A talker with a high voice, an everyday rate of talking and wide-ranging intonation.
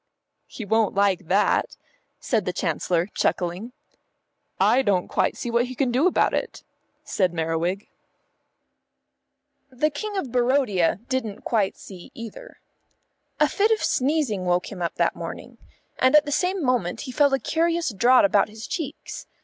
Yes: high, 235 Hz; average, 155 wpm; wide, 6.7 semitones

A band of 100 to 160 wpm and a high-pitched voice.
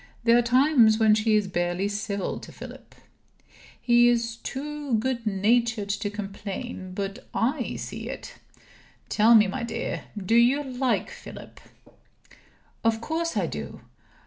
Yes: average, 140 wpm; high, 225 Hz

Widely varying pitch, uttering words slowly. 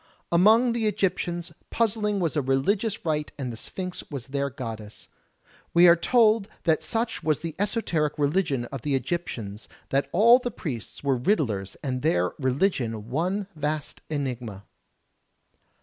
No: wide, 7.2 semitones; average, 145 wpm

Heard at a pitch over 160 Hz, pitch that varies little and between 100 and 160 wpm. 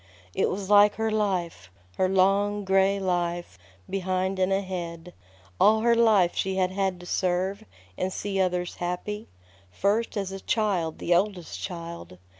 Yes: high, 190 Hz; narrow, 2.2 semitones; average, 150 wpm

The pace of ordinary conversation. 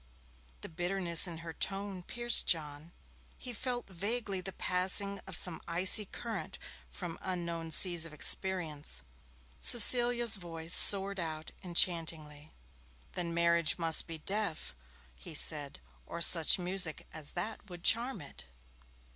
No: slow, 130 wpm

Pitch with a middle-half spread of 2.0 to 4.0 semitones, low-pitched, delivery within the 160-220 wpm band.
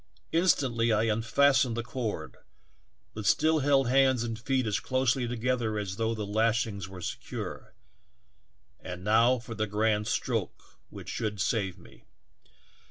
No: average, 3.2 semitones; low, 115 Hz; average, 140 wpm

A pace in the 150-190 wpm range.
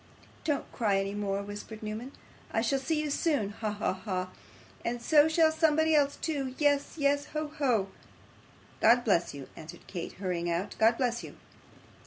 Yes: average, 170 wpm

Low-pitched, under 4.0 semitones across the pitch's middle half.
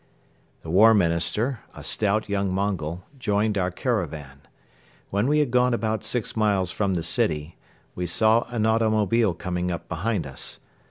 No: low, 100 Hz; average, 4.3 semitones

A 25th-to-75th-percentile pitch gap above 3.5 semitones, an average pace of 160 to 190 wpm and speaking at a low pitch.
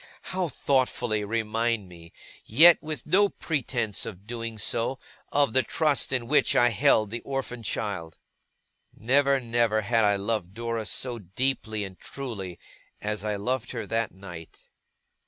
No: average, 4.0 semitones; average, 145 wpm; low, 115 Hz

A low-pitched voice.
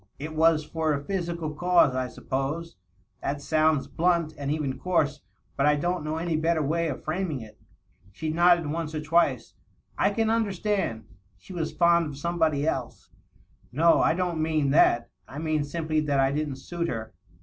No: medium, 155 Hz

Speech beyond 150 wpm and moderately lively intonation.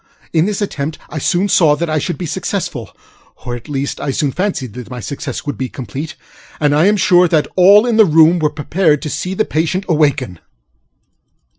Yes: average, 190 wpm; average, 4.4 semitones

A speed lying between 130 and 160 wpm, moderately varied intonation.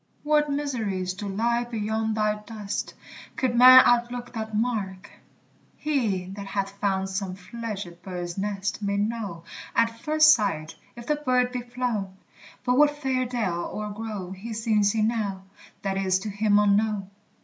Yes: average, 155 wpm; average, 3.5 semitones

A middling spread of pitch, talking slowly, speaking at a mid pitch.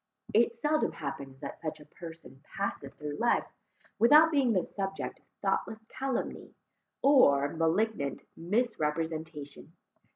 No: wide, 7.7 semitones; slow, 120 wpm; medium, 170 Hz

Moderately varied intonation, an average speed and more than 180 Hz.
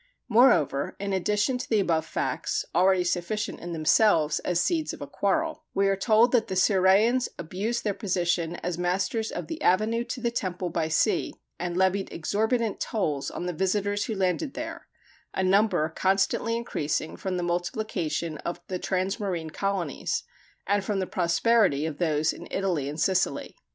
Yes: average, 3.7 semitones; average, 165 wpm; high, 190 Hz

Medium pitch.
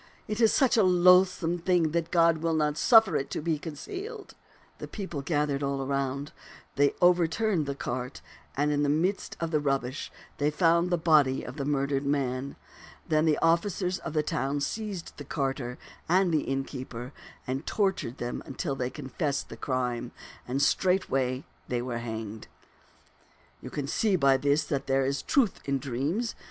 Yes: medium, 150 Hz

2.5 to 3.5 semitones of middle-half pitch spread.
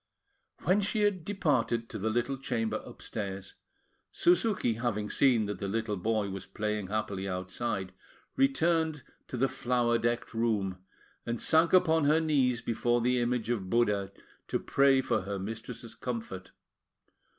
No: average, 4.6 semitones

